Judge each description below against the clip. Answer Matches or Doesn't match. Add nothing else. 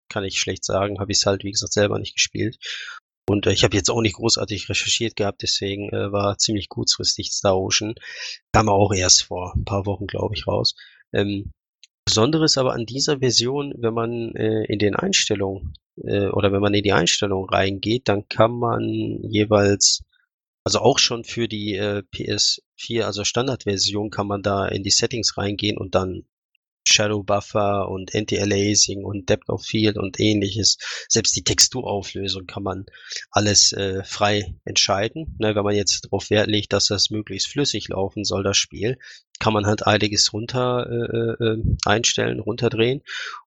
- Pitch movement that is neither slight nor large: Doesn't match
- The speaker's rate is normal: Matches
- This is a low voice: Matches